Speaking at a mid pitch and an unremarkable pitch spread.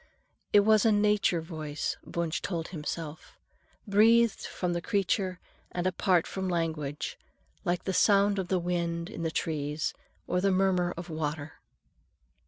Yes: medium, 175 Hz; average, 3.4 semitones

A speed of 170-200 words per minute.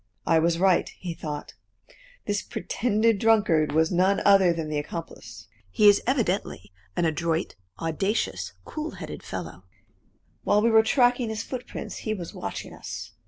No: average, 150 wpm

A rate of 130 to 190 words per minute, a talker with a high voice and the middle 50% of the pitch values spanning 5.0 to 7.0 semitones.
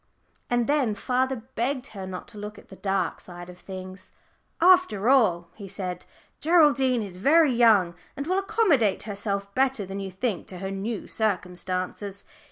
Yes: average, 165 wpm; high, 210 Hz; wide, 5.6 semitones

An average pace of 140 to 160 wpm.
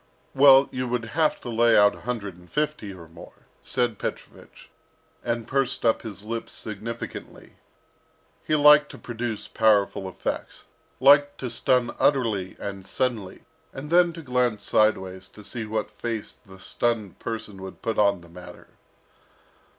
Yes: average, 150 wpm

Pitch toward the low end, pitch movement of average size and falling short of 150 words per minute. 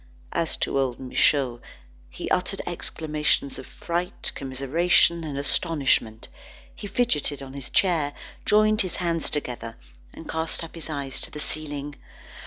No: medium, 150 Hz; average, 3.6 semitones; average, 140 wpm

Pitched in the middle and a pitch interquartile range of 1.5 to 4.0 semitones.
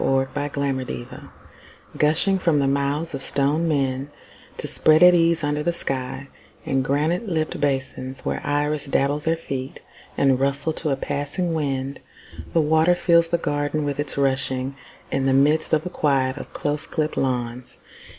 Yes: medium, 145 Hz; average, 2.7 semitones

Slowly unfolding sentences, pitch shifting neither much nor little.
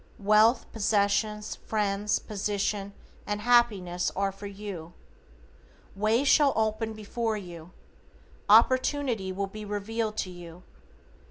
No: slow, 105 wpm; narrow, 2.1 semitones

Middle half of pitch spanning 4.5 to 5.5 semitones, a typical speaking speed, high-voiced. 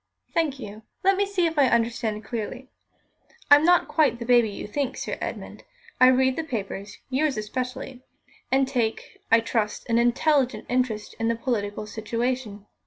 No: average, 3.4 semitones; average, 165 wpm; high, 245 Hz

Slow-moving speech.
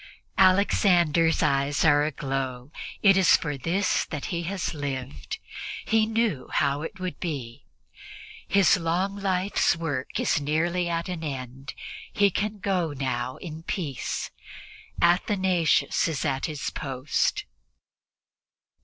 Yes: slow, 120 wpm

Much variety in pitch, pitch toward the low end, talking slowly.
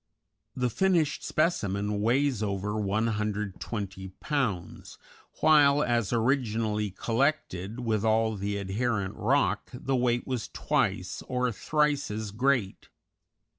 No: average, 4.5 semitones; low, 115 Hz; slow, 105 wpm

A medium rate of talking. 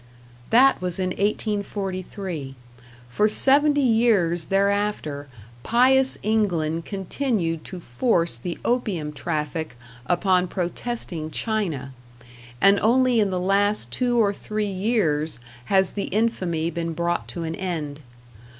No: slow, 115 wpm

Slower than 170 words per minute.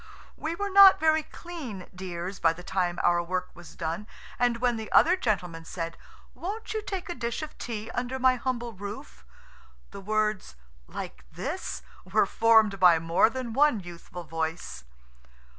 Yes: average, 160 wpm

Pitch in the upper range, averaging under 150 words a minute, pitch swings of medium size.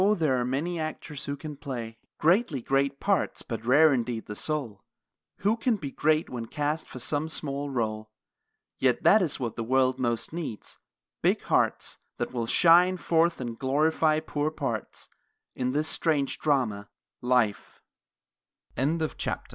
No: medium, 140 Hz; slow, 135 wpm; average, 4.3 semitones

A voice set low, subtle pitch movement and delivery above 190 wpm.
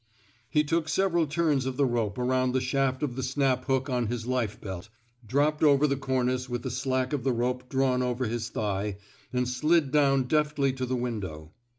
Yes: low, 130 Hz; narrow, 2.3 semitones; average, 200 wpm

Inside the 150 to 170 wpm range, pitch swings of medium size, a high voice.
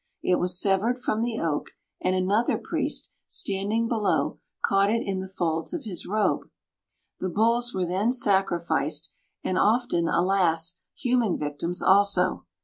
No: average, 140 wpm; average, 3.9 semitones; high, 195 Hz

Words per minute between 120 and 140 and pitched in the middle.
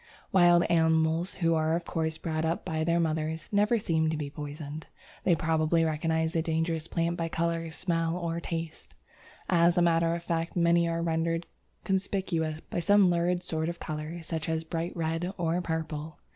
No: average, 175 wpm; medium, 165 Hz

